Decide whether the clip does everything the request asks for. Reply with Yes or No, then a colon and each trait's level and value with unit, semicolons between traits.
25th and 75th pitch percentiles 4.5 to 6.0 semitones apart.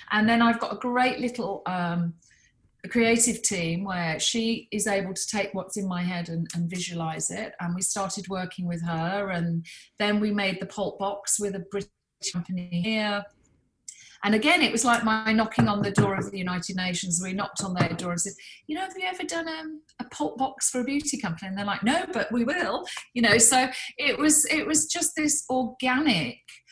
Yes: average, 5.2 semitones